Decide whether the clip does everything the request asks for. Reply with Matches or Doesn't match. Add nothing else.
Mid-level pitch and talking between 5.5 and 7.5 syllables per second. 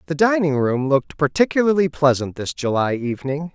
Matches